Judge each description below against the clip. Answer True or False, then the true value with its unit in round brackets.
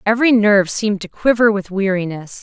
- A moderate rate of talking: True (175 wpm)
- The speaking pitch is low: False (205 Hz)